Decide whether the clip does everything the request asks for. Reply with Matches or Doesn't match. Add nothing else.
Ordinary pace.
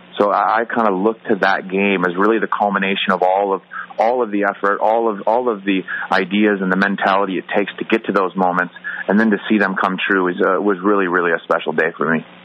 Doesn't match